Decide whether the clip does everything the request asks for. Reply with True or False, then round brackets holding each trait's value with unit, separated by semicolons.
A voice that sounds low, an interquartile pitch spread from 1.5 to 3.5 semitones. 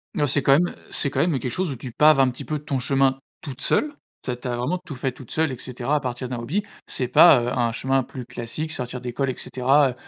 True (130 Hz; 2.7 semitones)